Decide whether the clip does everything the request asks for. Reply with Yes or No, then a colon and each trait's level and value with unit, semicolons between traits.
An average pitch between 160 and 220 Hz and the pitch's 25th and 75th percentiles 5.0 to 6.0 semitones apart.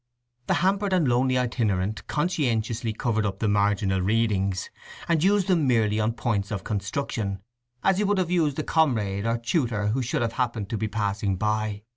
No: low, 115 Hz; wide, 5.4 semitones